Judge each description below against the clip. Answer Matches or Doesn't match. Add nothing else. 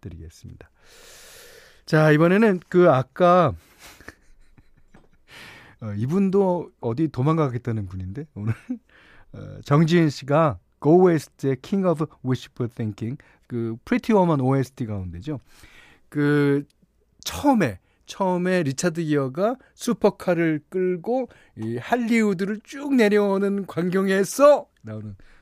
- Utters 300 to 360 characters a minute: Doesn't match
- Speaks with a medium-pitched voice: Matches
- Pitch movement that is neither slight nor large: Doesn't match